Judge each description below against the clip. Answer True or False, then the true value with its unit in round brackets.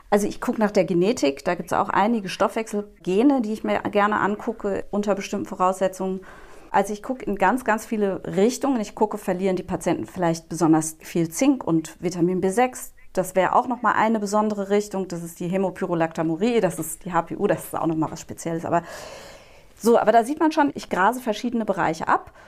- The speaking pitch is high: True (195 Hz)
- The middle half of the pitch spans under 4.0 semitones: True (3.5 semitones)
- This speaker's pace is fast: True (200 wpm)